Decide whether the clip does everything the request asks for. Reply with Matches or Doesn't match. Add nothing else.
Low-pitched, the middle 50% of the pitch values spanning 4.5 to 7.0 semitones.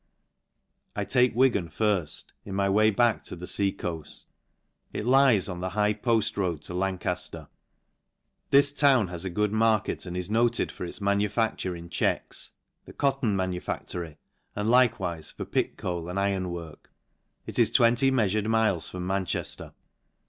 Doesn't match